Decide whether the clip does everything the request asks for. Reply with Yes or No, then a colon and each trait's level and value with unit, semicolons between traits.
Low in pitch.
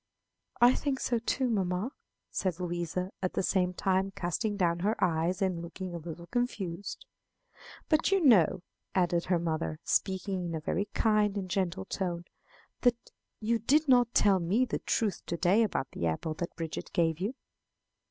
No: medium, 185 Hz